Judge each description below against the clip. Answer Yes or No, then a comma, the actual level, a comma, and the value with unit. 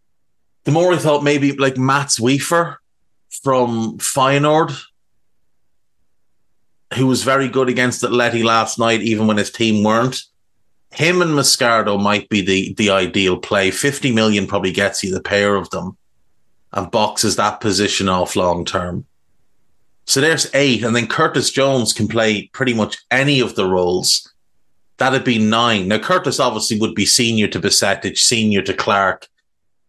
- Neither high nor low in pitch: No, low, 115 Hz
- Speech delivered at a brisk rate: No, average, 155 wpm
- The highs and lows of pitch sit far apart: No, average, 4.7 semitones